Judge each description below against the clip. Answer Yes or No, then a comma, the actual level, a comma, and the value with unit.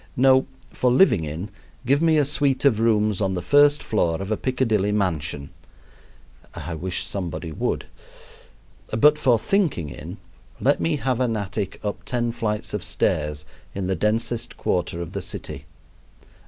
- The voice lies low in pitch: Yes, low, 105 Hz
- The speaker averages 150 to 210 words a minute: Yes, average, 155 wpm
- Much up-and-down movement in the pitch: Yes, wide, 6.2 semitones